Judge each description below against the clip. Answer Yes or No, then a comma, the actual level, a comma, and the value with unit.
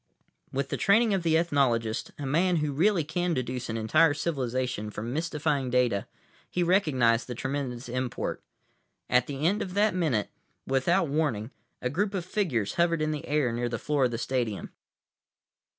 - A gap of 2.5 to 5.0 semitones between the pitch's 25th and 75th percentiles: No, wide, 5.5 semitones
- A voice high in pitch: No, medium, 140 Hz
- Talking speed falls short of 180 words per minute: Yes, average, 170 wpm